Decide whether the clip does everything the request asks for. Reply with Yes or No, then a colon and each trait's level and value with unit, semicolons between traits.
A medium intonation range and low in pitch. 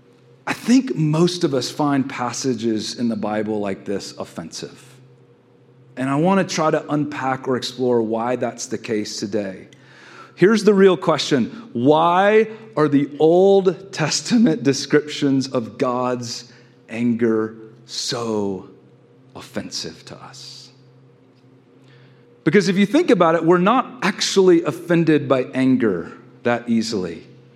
No: wide, 5.8 semitones; low, 130 Hz